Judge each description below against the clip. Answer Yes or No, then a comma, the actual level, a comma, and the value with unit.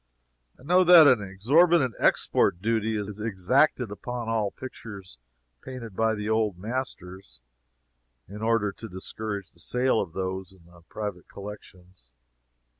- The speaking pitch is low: Yes, low, 105 Hz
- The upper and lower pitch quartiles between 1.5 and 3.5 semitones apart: No, average, 3.9 semitones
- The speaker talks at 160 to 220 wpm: No, slow, 135 wpm